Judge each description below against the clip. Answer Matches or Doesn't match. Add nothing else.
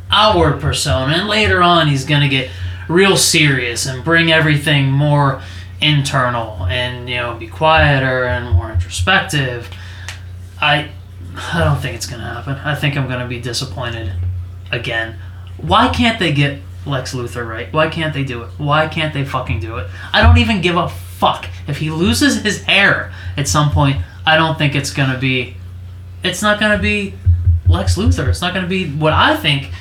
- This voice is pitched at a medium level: Doesn't match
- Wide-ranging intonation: Matches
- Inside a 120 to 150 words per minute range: Doesn't match